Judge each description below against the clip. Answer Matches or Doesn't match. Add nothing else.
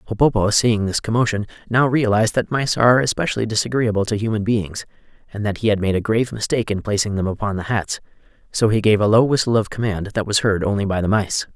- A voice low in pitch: Matches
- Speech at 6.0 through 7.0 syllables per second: Matches